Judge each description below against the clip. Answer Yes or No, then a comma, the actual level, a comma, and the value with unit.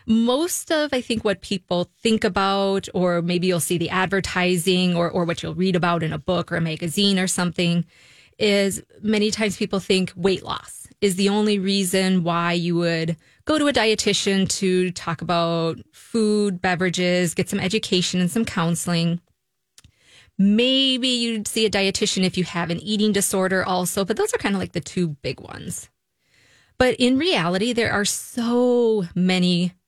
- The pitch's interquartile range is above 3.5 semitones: No, average, 3.2 semitones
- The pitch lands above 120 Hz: Yes, high, 190 Hz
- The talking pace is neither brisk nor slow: Yes, average, 175 wpm